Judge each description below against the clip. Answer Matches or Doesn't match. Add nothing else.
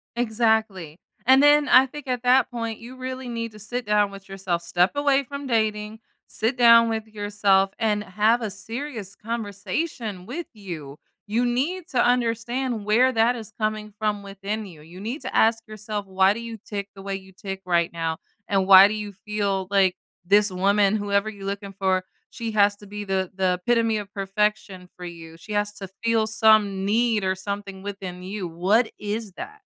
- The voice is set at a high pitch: Matches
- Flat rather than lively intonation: Doesn't match